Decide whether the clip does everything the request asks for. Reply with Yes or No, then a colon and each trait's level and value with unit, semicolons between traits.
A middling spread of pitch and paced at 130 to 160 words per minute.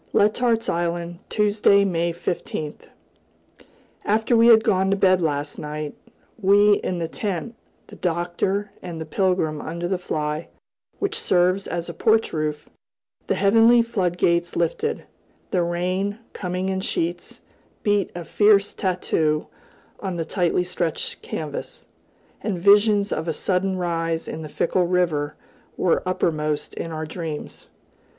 Yes: average, 3.3 semitones; slow, 135 wpm